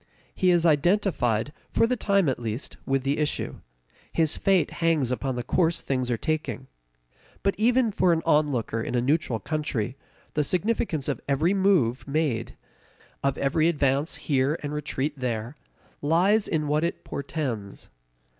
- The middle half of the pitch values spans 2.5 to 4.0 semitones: No, average, 4.5 semitones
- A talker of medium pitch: Yes, medium, 150 Hz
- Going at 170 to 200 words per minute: No, average, 155 wpm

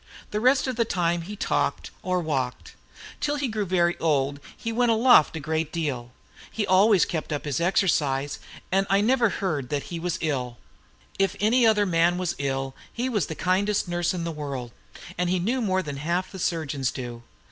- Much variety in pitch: Yes, wide, 5.8 semitones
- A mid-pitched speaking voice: Yes, medium, 175 Hz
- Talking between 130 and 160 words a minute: No, average, 195 wpm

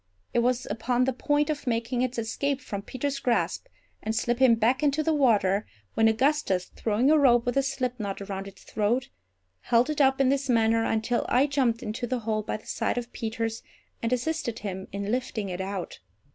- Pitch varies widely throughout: No, average, 3.4 semitones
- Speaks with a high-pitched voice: Yes, high, 235 Hz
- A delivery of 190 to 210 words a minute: Yes, average, 195 wpm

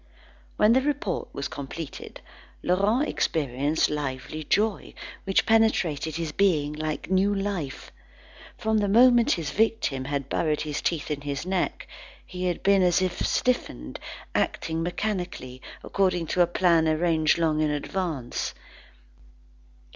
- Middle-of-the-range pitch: Yes, medium, 170 Hz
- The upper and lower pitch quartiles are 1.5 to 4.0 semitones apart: No, average, 4.9 semitones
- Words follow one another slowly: Yes, slow, 130 wpm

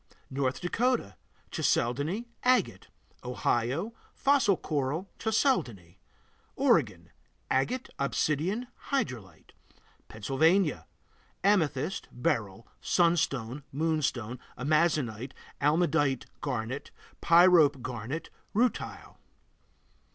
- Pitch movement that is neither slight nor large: No, wide, 6.2 semitones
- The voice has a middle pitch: Yes, medium, 150 Hz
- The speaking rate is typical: No, slow, 70 wpm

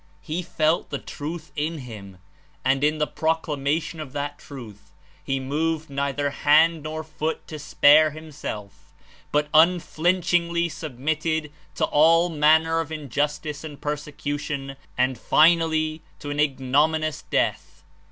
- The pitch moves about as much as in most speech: No, narrow, 1.9 semitones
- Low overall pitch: No, medium, 155 Hz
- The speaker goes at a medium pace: No, slow, 130 wpm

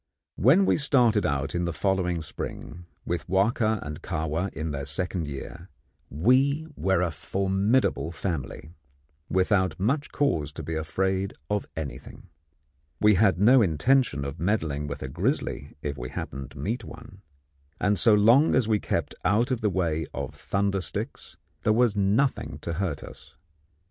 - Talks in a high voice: No, very low, 95 Hz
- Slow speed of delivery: No, average, 160 wpm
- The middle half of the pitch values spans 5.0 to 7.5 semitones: Yes, wide, 5.6 semitones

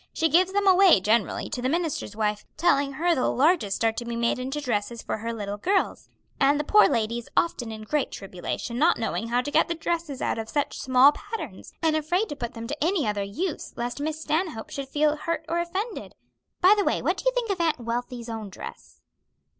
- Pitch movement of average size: No, wide, 6.5 semitones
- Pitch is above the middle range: Yes, very high, 280 Hz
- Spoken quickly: Yes, fast, 225 wpm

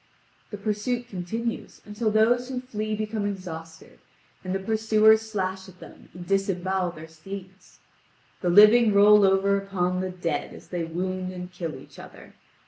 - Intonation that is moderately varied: Yes, average, 3.0 semitones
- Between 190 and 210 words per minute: No, average, 155 wpm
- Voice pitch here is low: No, high, 195 Hz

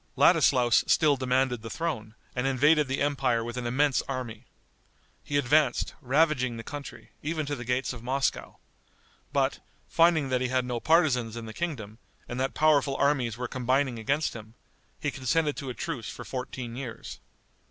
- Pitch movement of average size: Yes, average, 3.1 semitones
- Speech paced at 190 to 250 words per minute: No, average, 170 wpm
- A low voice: Yes, low, 130 Hz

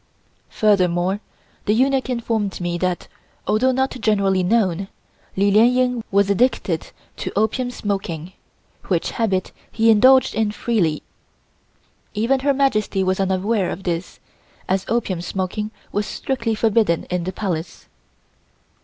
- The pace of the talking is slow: Yes, slow, 130 wpm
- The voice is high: Yes, high, 205 Hz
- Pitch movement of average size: Yes, average, 3.7 semitones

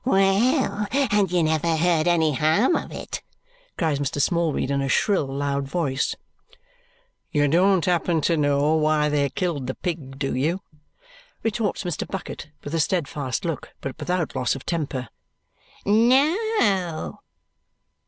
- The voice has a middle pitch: Yes, medium, 165 Hz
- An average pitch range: Yes, average, 5.0 semitones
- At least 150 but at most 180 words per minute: No, average, 140 wpm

